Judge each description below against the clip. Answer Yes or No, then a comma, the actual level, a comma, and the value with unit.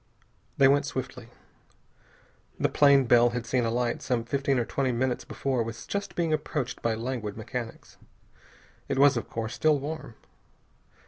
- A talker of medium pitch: No, low, 125 Hz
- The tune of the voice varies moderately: Yes, average, 3.1 semitones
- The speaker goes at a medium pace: Yes, average, 150 wpm